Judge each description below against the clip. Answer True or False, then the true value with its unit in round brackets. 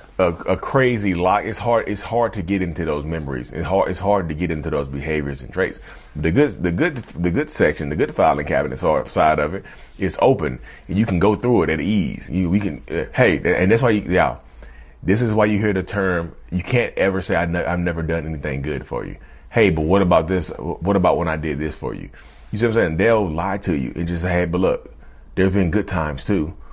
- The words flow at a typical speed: False (250 wpm)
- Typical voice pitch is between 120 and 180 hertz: False (90 Hz)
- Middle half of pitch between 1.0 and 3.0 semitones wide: False (4.3 semitones)